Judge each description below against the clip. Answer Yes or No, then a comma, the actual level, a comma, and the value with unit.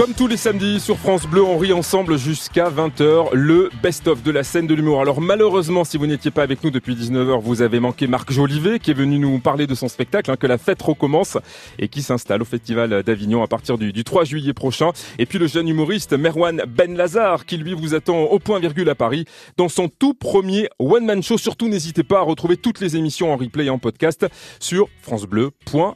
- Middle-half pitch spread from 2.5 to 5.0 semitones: No, wide, 5.6 semitones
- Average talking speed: No, fast, 225 wpm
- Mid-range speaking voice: Yes, medium, 155 Hz